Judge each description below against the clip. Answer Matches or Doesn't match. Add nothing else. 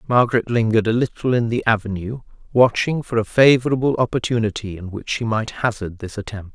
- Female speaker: Doesn't match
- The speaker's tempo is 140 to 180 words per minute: Matches